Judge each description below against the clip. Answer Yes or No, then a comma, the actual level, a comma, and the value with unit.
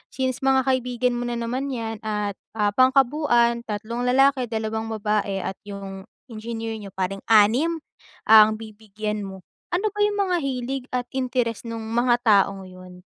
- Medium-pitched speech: No, high, 230 Hz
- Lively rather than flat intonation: No, average, 3.4 semitones